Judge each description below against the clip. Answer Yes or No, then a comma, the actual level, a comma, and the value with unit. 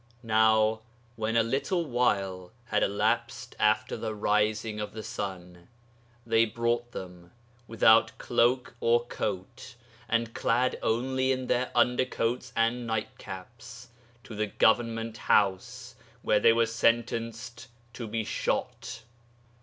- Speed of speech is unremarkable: No, slow, 120 wpm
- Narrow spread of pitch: Yes, narrow, 1.9 semitones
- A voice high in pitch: No, low, 115 Hz